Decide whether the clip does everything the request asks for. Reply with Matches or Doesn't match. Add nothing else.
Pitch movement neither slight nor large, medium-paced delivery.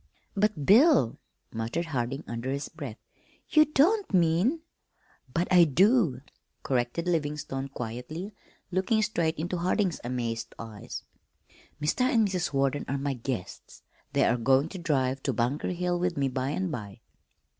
Doesn't match